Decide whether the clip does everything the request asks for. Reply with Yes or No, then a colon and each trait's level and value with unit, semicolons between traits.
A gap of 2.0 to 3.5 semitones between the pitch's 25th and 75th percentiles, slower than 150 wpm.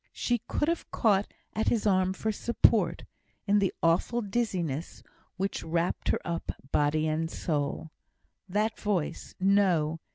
No: average, 4.5 semitones; slow, 135 wpm